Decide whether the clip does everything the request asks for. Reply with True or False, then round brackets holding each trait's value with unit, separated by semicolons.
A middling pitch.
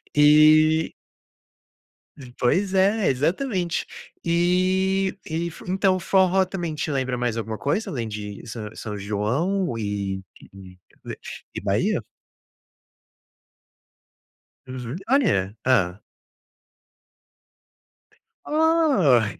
True (155 Hz)